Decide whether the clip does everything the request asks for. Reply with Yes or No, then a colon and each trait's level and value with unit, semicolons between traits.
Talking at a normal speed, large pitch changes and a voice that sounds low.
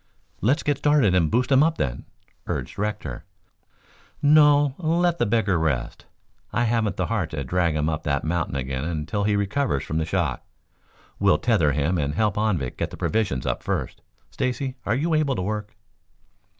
Yes: average, 175 wpm; wide, 8.8 semitones; low, 105 Hz